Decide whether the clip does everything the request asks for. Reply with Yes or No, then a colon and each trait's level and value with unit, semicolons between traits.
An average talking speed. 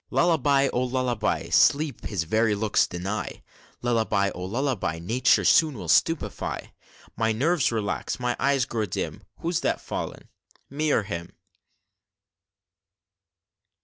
No: slow, 120 wpm